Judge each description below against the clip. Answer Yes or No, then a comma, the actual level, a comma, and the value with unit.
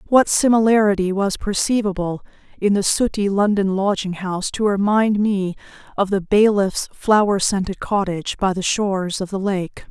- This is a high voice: Yes, high, 200 Hz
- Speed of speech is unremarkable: Yes, average, 150 wpm